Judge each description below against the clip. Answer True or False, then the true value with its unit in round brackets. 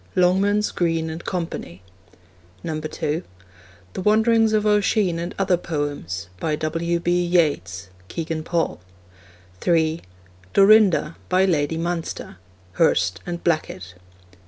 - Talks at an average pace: False (110 wpm)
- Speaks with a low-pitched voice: False (165 Hz)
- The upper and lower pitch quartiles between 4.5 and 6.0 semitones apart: False (3.7 semitones)